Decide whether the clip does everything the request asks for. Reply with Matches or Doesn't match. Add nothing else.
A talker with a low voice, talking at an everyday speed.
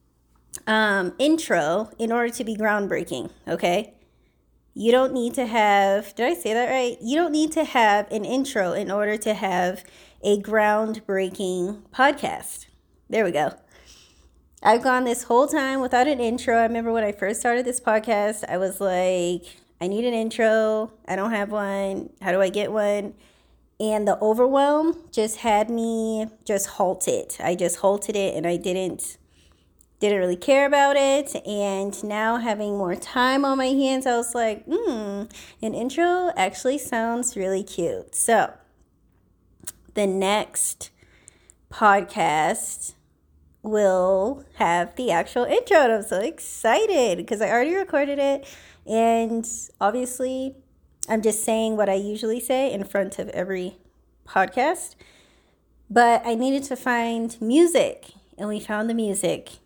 Doesn't match